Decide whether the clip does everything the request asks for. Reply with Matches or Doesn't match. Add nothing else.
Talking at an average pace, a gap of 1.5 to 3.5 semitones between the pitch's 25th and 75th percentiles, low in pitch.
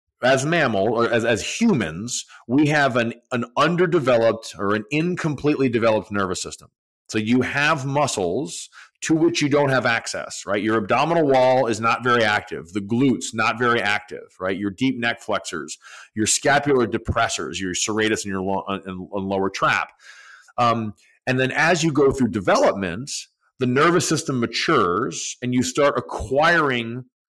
Doesn't match